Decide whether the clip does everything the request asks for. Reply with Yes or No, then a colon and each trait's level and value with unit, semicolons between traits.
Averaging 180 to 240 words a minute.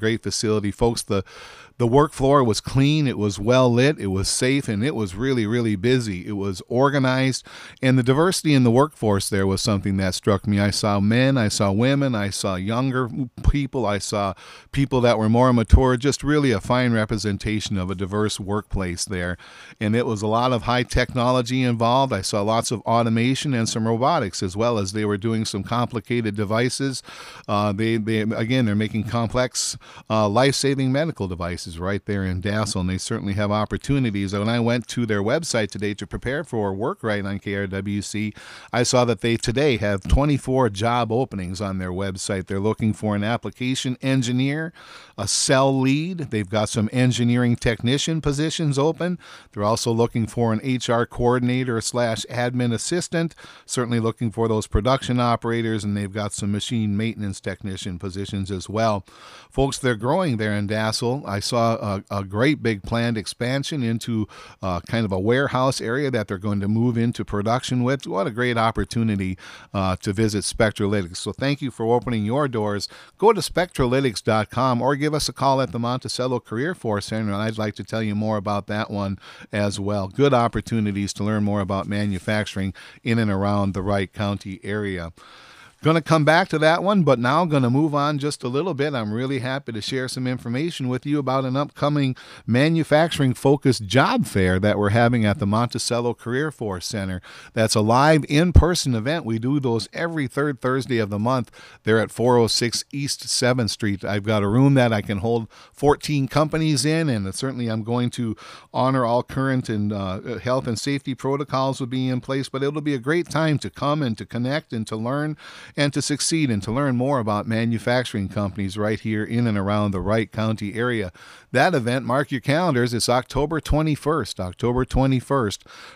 Yes: average, 185 wpm